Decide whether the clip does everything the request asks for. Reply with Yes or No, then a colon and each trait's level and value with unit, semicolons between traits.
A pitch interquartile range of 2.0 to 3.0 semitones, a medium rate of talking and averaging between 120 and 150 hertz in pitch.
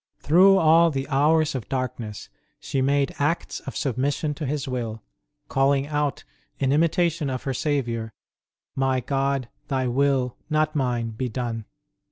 Yes: average, 2.7 semitones; average, 145 wpm; low, 135 Hz